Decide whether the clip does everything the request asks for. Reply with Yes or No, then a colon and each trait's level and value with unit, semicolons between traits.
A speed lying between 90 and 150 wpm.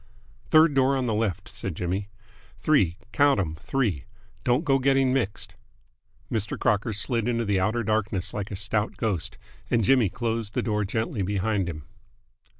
No: average, 160 wpm